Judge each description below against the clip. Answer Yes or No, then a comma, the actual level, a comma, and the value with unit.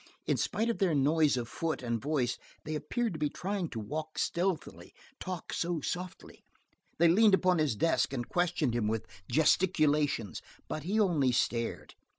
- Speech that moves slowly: No, average, 165 wpm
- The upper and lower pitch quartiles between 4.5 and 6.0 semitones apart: Yes, average, 5.2 semitones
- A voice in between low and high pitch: Yes, medium, 155 Hz